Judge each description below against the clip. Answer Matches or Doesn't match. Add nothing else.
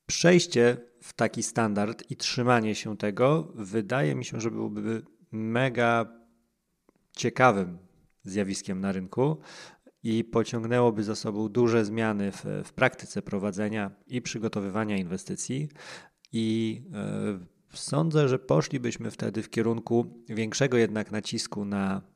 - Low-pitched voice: Matches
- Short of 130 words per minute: Matches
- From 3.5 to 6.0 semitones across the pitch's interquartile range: Doesn't match